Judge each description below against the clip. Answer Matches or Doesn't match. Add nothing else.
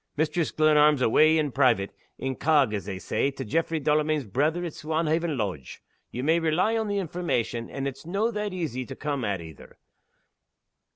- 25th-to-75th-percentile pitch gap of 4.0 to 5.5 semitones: Matches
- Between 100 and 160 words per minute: Doesn't match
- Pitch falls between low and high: Matches